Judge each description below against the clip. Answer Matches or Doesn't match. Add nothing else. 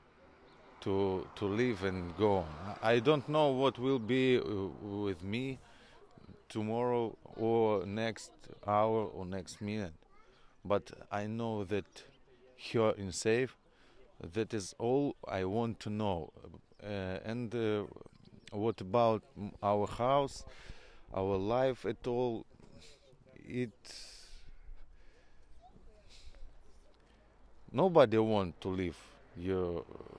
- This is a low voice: Matches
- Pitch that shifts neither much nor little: Matches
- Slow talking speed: Matches